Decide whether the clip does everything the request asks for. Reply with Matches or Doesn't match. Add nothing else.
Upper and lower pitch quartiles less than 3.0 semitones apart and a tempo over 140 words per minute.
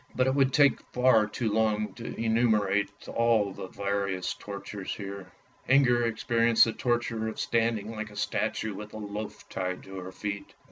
Matches